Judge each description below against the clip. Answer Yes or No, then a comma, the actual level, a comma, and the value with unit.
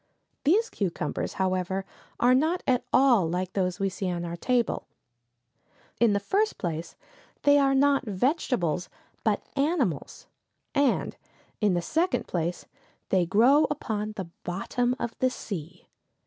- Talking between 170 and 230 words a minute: No, slow, 135 wpm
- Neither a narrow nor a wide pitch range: No, wide, 7.2 semitones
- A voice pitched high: Yes, high, 210 Hz